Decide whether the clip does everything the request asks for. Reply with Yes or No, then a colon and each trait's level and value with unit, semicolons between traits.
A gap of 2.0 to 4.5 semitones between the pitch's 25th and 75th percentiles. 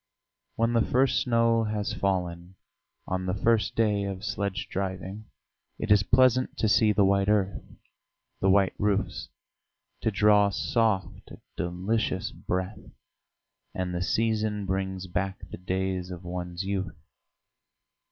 Yes: narrow, 2.6 semitones